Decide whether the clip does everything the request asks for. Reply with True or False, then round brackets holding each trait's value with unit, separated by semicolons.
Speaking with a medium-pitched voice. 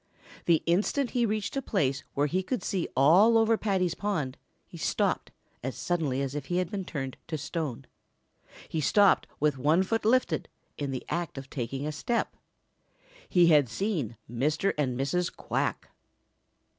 True (165 Hz)